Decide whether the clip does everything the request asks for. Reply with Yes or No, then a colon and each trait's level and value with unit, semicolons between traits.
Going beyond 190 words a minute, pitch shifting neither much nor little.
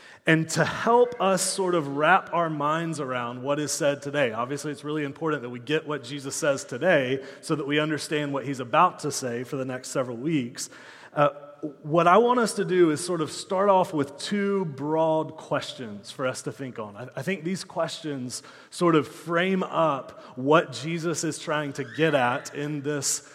Yes: average, 200 wpm; average, 3.1 semitones